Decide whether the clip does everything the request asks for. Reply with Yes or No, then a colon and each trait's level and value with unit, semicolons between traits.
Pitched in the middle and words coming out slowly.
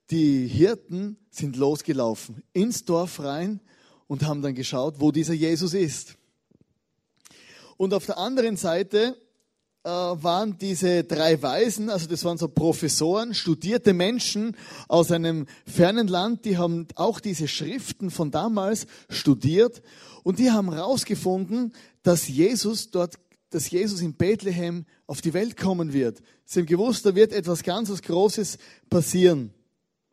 No: medium, 180 Hz; average, 135 wpm